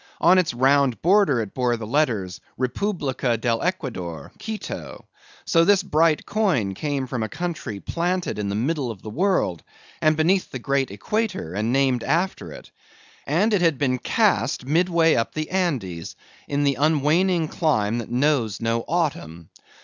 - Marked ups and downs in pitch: Yes, wide, 6.9 semitones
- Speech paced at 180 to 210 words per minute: No, average, 160 wpm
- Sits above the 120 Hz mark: Yes, medium, 140 Hz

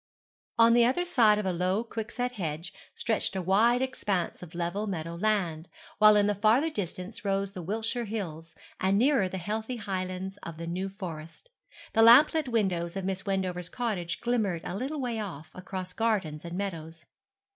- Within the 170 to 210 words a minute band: Yes, average, 180 wpm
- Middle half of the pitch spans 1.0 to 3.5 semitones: No, average, 4.1 semitones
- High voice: Yes, high, 195 Hz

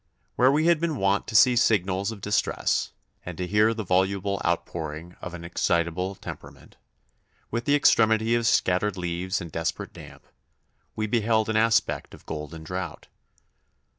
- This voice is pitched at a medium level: No, low, 100 Hz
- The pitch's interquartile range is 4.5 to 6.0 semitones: No, average, 4.1 semitones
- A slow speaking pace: No, average, 155 wpm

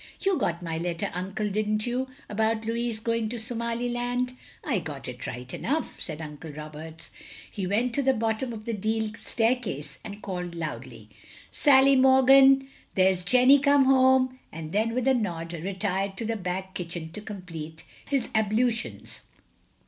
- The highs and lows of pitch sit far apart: Yes, wide, 6.1 semitones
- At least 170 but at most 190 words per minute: No, average, 155 wpm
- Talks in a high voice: Yes, high, 215 Hz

